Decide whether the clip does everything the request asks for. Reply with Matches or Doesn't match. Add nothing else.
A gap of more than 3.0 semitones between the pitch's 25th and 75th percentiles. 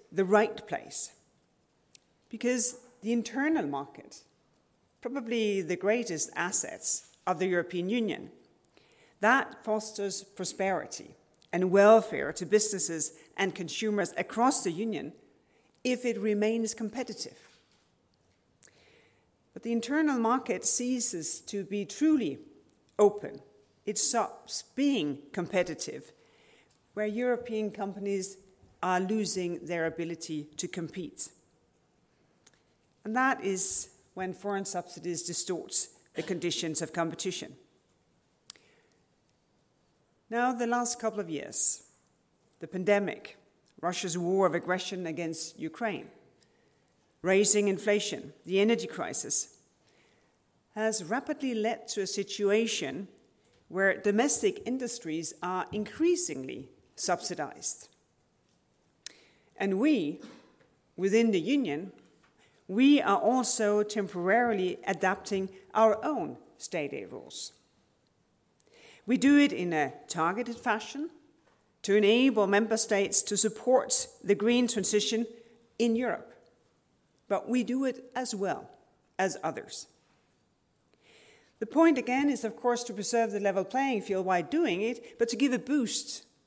Matches